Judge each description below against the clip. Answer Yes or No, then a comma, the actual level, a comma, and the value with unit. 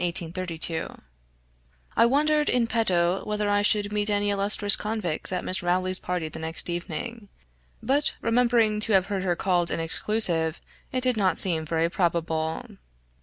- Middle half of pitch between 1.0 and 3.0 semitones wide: No, average, 4.2 semitones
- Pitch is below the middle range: No, high, 195 Hz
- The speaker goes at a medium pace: Yes, average, 155 wpm